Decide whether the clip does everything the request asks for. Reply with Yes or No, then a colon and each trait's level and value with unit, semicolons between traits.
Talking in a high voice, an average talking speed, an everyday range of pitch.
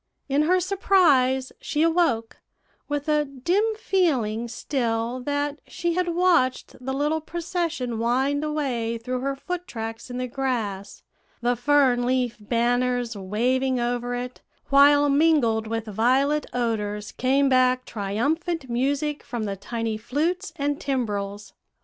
No: very high, 255 Hz; slow, 130 wpm; average, 4.1 semitones